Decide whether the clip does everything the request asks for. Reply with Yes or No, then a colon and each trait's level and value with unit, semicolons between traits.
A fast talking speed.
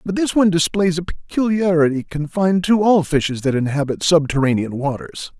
No: average, 155 wpm